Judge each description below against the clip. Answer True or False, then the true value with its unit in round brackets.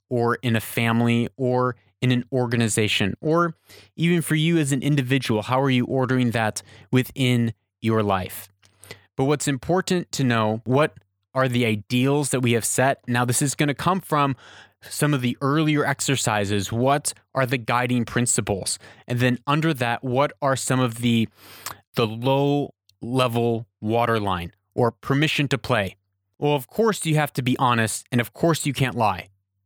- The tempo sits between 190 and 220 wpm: False (170 wpm)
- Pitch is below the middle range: True (125 Hz)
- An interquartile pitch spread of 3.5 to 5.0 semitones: True (3.9 semitones)